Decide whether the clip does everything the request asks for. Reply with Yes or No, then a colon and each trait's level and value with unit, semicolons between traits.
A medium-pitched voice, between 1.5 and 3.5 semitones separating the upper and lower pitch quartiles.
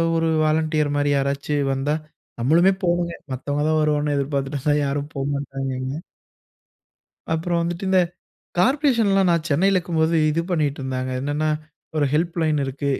Yes: medium, 150 Hz; average, 3.2 semitones